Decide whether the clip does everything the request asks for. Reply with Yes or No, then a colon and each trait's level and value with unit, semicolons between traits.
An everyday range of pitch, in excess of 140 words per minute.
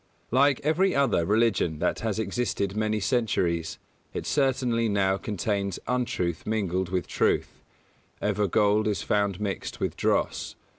No: average, 3.4 semitones; slow, 135 wpm